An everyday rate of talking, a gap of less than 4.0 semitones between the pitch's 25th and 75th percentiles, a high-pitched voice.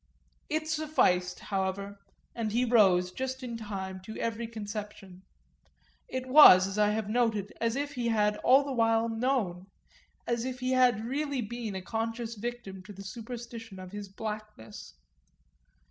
Yes: average, 160 wpm; average, 3.6 semitones; high, 225 Hz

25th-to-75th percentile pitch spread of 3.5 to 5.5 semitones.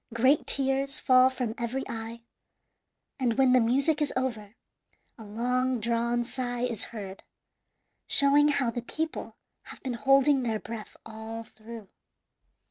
No: average, 2.8 semitones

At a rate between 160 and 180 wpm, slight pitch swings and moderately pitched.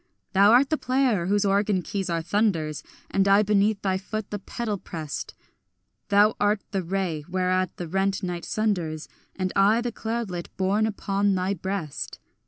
No: average, 165 wpm; narrow, 2.3 semitones; high, 195 Hz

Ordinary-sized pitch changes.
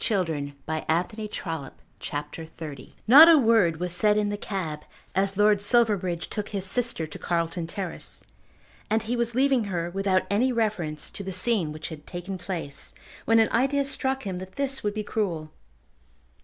Yes: average, 5.0 semitones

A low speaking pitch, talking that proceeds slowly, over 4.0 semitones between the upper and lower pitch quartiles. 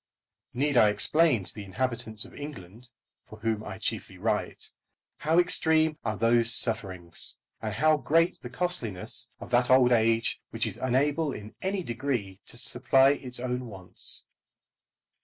No: low, 125 Hz; average, 150 wpm; average, 5.0 semitones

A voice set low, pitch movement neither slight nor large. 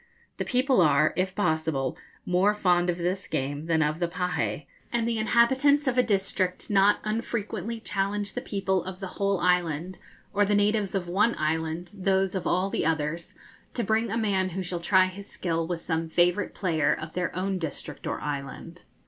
No: medium, 185 Hz; average, 3.7 semitones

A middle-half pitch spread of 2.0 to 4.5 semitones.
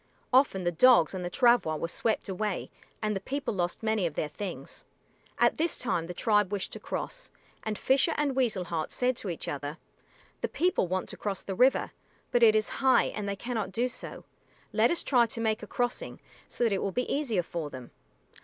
No: wide, 5.5 semitones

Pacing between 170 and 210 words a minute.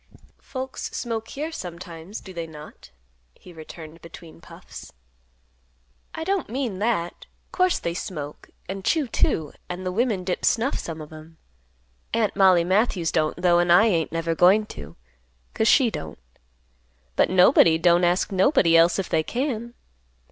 No: average, 155 wpm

